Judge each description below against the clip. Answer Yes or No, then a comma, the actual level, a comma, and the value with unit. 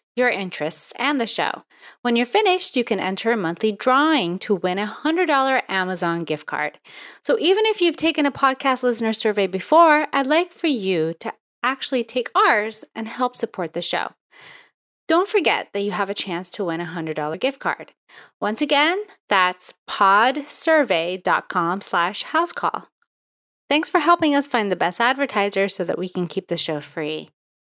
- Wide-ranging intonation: Yes, wide, 8.1 semitones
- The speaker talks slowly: No, average, 170 wpm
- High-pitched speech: Yes, high, 230 Hz